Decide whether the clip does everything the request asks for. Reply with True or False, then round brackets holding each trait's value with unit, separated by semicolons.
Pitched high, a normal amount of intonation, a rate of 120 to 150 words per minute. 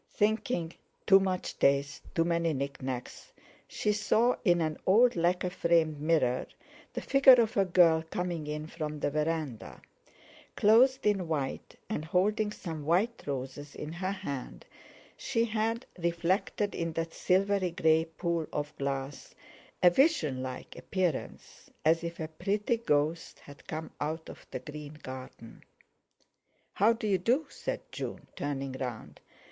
False (165 Hz; 4.9 semitones; 140 wpm)